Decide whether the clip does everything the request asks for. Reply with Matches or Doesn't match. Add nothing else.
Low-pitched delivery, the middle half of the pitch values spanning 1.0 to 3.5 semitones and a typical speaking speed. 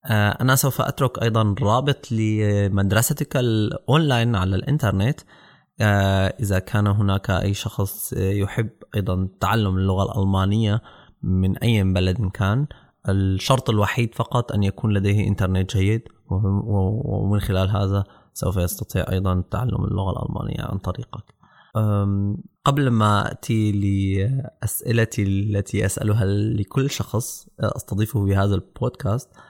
Doesn't match